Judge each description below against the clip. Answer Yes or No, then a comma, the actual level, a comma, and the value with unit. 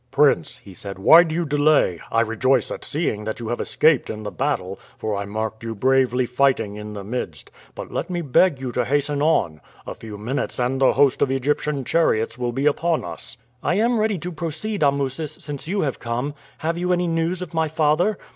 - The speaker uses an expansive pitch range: Yes, wide, 6.0 semitones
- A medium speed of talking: No, fast, 210 wpm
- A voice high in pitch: No, medium, 140 Hz